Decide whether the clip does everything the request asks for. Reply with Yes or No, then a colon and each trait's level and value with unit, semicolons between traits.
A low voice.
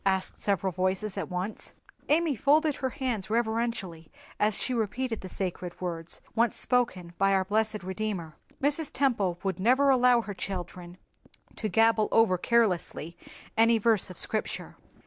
No: high, 215 Hz